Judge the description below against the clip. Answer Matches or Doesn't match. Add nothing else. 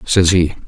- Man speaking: Matches